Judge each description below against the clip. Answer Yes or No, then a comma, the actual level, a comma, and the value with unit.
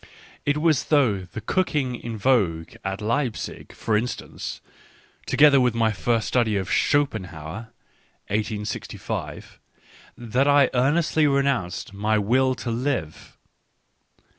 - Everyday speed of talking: No, slow, 115 wpm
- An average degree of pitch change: Yes, average, 4.7 semitones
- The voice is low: Yes, low, 120 Hz